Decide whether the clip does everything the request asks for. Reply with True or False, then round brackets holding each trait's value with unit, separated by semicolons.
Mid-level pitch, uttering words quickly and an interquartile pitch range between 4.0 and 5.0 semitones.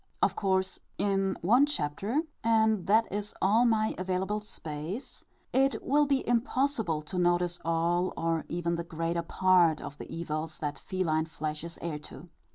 False (180 Hz; 160 wpm; 4.7 semitones)